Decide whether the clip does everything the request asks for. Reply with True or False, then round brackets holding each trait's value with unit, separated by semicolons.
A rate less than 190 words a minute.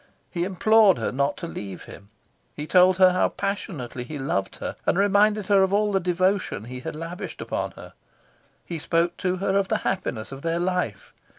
False (195 wpm)